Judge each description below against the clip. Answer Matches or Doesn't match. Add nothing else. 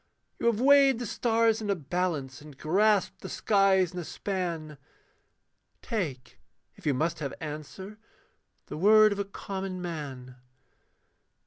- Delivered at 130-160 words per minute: Matches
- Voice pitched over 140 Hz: Matches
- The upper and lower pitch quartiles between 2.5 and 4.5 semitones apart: Doesn't match